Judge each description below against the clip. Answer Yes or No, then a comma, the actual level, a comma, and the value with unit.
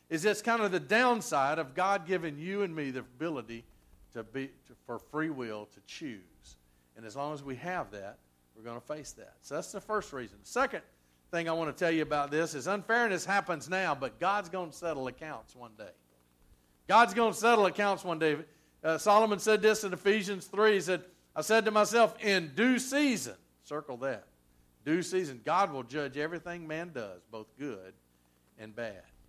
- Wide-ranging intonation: Yes, wide, 9.0 semitones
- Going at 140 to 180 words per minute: No, average, 200 wpm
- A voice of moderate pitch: Yes, medium, 160 Hz